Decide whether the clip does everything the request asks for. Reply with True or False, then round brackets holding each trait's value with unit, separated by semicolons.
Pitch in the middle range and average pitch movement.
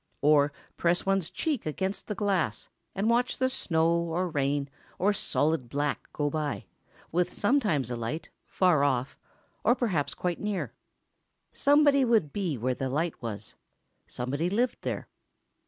False (170 Hz; 6.3 semitones)